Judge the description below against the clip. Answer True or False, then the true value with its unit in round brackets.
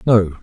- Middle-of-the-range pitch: False (100 Hz)